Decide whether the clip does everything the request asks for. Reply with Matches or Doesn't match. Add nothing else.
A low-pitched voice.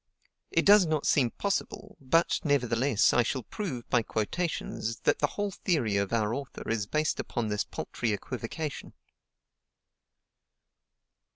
Matches